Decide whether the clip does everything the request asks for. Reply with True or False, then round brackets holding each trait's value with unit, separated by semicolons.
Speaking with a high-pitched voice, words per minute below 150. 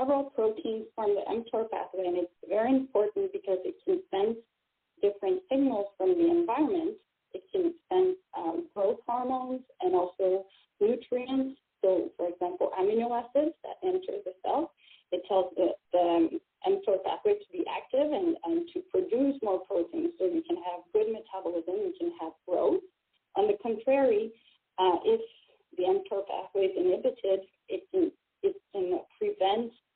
False (255 Hz; 155 wpm)